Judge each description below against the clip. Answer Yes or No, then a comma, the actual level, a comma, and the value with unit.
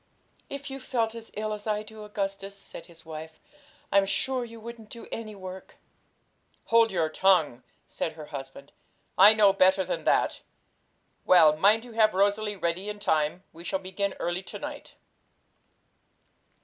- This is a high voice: Yes, high, 200 Hz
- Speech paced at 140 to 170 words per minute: Yes, average, 160 wpm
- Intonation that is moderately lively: Yes, average, 3.9 semitones